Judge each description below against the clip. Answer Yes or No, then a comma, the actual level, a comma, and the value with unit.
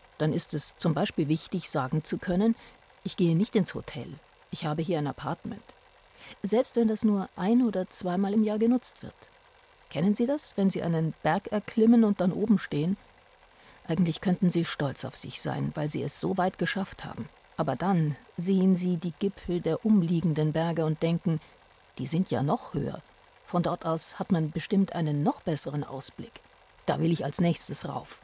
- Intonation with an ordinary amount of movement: Yes, average, 3.9 semitones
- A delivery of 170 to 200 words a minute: Yes, average, 185 wpm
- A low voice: No, medium, 180 Hz